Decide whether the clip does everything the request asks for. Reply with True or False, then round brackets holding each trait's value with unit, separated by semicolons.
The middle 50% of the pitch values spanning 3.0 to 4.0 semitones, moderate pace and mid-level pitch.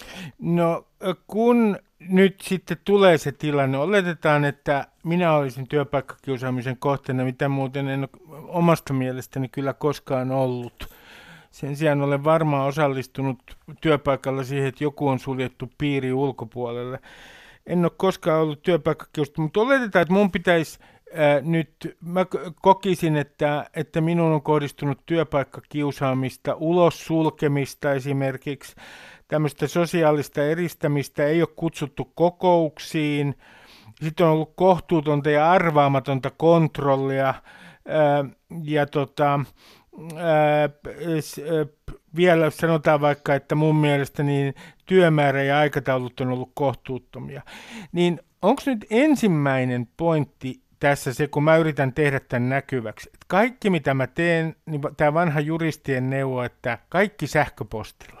True (3.4 semitones; 115 wpm; 150 Hz)